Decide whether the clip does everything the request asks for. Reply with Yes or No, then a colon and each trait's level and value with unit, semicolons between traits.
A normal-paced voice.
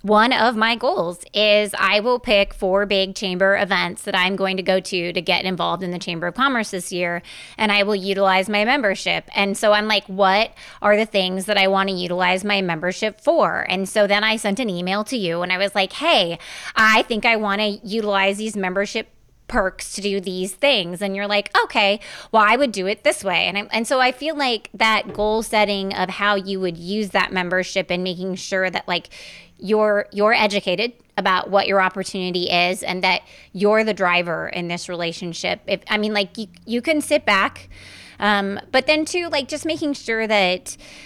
No: fast, 210 wpm